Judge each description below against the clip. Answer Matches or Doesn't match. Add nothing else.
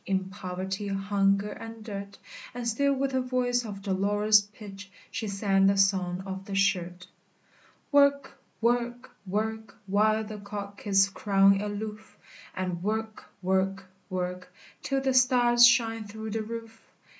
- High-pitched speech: Matches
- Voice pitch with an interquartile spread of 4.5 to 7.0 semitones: Doesn't match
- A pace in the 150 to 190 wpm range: Doesn't match